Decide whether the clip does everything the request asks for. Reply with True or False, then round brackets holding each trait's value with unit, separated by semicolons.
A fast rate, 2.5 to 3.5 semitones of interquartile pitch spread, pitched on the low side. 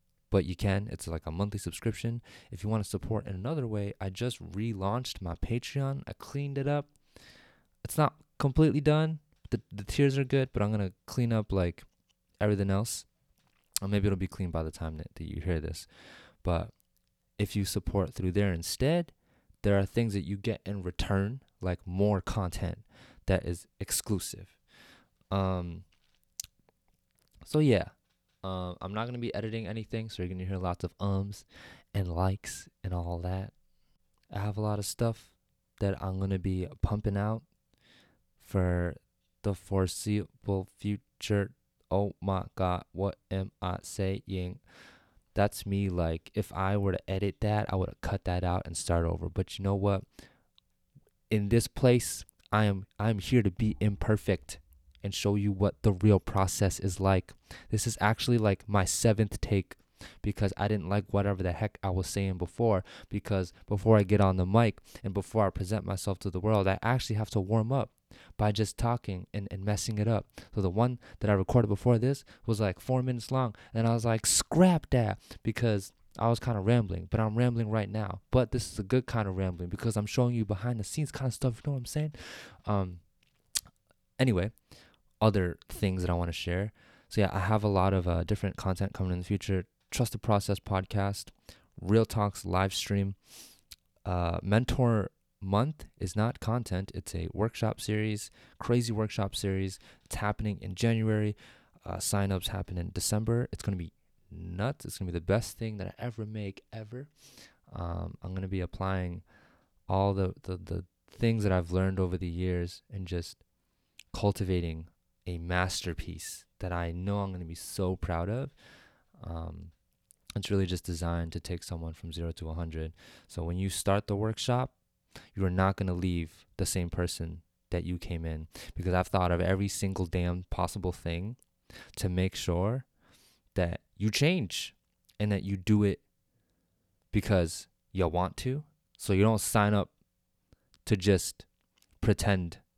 False (180 wpm; 3.2 semitones; 100 Hz)